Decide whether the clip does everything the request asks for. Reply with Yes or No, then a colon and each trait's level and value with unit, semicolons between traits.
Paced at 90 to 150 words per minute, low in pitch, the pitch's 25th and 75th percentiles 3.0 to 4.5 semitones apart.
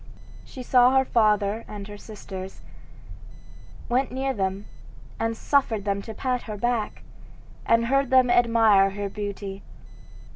No: slow, 135 wpm; high, 225 Hz; average, 3.5 semitones